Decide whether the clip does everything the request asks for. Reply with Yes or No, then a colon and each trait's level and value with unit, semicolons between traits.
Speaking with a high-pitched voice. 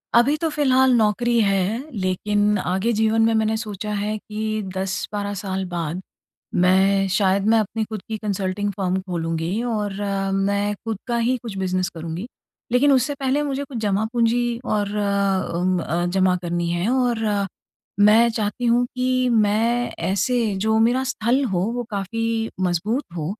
Yes: high, 210 Hz